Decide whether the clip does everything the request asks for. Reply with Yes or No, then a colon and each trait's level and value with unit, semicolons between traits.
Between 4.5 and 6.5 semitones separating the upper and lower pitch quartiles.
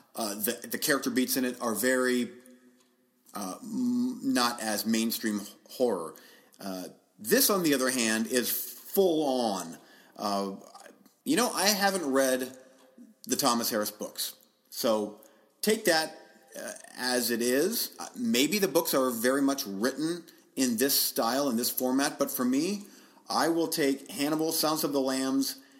Yes: average, 5.1 semitones